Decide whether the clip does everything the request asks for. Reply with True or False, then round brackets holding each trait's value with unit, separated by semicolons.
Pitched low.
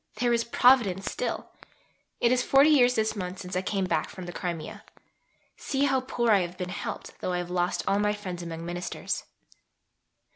False (195 Hz)